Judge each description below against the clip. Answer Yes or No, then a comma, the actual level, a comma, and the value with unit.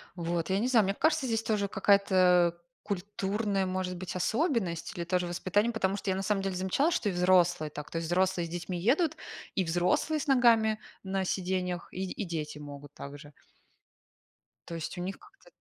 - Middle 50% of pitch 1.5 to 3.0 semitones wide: No, average, 3.4 semitones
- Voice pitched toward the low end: No, high, 190 Hz